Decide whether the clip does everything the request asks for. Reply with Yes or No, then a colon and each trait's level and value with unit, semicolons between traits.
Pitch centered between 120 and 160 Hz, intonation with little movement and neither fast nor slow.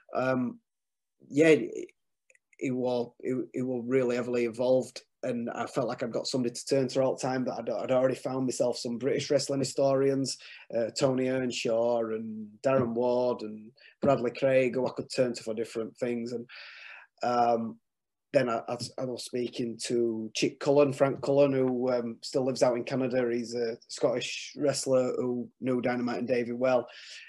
Yes: low, 125 Hz; narrow, 1.8 semitones; average, 170 wpm